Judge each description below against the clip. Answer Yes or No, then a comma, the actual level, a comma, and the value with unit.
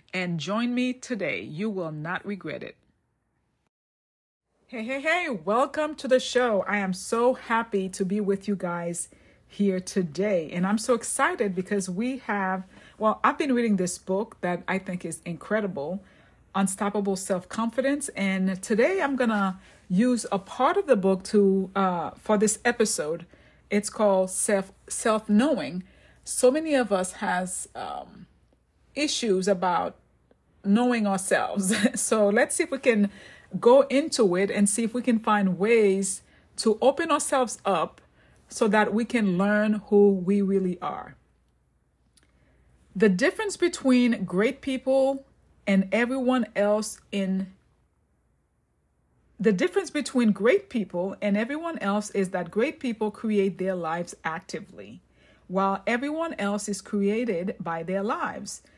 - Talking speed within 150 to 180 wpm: No, average, 140 wpm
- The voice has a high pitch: Yes, high, 205 Hz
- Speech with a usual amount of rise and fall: Yes, average, 4.2 semitones